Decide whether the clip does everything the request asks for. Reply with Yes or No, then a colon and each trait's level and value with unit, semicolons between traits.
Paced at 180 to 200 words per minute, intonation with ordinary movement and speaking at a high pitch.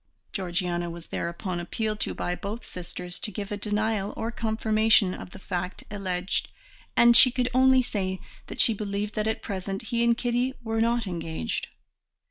No: average, 170 wpm; average, 3.8 semitones; high, 205 Hz